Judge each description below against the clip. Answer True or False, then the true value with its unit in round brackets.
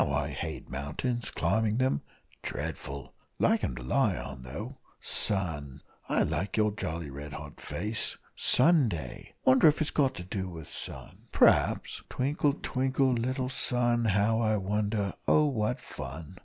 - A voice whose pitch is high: False (105 Hz)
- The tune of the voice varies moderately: False (8.0 semitones)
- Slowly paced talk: False (145 wpm)